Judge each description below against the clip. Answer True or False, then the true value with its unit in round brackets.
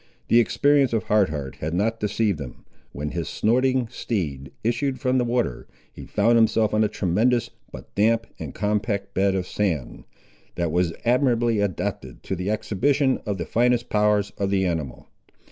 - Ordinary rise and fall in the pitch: True (4.6 semitones)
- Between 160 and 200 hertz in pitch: False (105 Hz)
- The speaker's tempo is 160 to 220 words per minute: True (170 wpm)